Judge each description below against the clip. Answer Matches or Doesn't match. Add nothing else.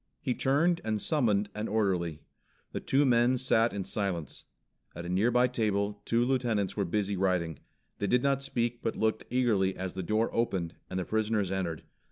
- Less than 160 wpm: Doesn't match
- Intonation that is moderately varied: Matches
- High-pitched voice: Doesn't match